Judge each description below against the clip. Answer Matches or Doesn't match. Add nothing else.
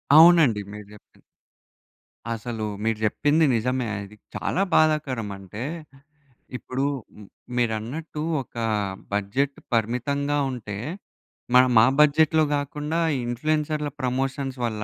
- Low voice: Matches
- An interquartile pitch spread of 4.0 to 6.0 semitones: Matches